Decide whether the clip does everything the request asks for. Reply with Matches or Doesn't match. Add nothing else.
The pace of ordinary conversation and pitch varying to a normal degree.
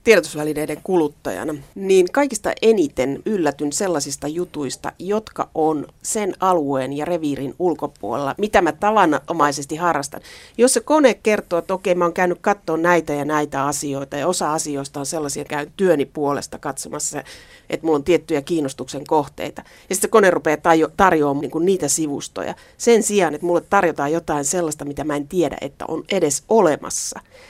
Doesn't match